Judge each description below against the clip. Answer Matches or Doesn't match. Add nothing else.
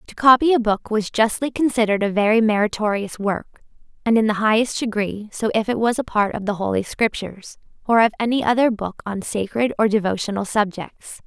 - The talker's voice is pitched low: Doesn't match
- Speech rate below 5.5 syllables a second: Doesn't match